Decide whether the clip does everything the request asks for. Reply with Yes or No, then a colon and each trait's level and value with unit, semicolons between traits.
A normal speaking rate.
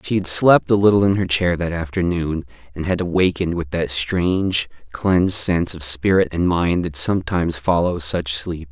Yes: average, 185 wpm